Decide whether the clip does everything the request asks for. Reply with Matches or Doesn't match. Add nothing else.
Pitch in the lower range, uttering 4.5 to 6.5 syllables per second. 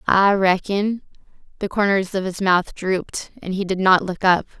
Doesn't match